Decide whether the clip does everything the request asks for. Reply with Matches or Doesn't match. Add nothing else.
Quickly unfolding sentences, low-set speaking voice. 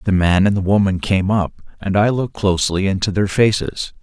Matches